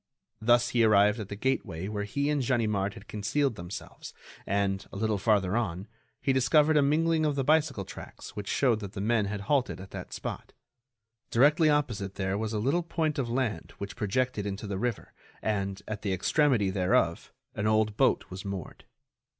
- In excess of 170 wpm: Yes, average, 185 wpm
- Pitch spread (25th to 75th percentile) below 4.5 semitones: No, average, 5.0 semitones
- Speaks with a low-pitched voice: Yes, low, 110 Hz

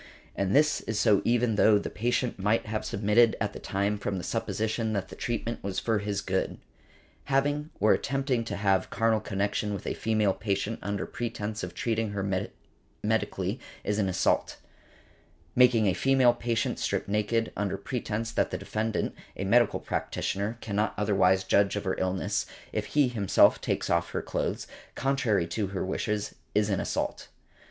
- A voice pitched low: Yes, low, 105 Hz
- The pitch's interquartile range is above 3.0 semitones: No, narrow, 2.6 semitones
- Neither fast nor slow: Yes, average, 170 wpm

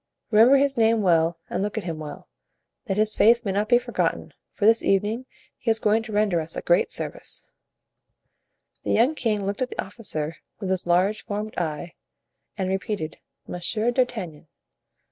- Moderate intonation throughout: Yes, average, 4.1 semitones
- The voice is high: Yes, high, 210 Hz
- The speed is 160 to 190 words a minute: Yes, average, 175 wpm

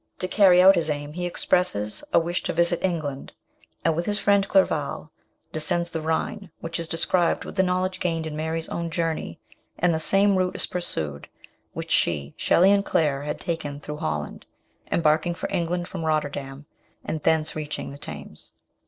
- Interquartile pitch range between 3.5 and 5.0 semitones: No, average, 3.1 semitones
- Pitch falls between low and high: Yes, medium, 165 Hz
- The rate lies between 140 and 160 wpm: No, average, 180 wpm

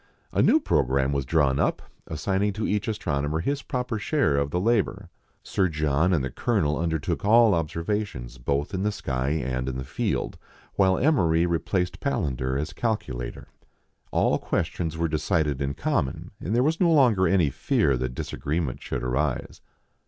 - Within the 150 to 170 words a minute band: Yes, average, 165 wpm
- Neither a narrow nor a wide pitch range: No, wide, 6.7 semitones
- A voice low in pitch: Yes, very low, 80 Hz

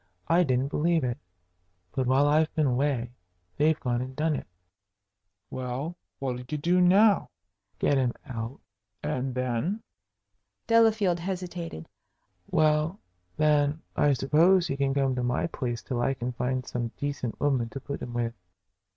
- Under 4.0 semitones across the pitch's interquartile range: No, average, 4.3 semitones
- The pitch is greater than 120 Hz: Yes, medium, 140 Hz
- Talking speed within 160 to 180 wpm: No, average, 150 wpm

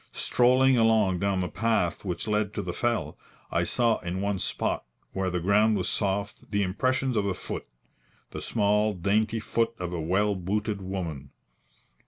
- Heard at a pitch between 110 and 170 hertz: No, low, 100 Hz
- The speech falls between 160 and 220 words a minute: Yes, average, 170 wpm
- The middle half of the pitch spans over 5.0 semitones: No, average, 2.9 semitones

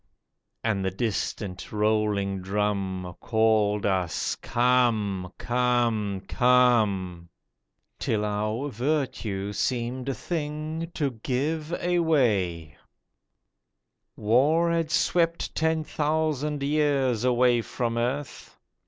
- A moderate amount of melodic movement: No, wide, 6.0 semitones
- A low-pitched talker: Yes, low, 120 Hz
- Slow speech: Yes, slow, 90 wpm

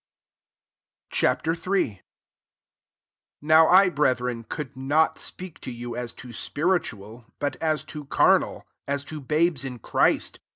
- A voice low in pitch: No, medium, 145 Hz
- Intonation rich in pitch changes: No, average, 4.5 semitones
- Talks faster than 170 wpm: No, slow, 135 wpm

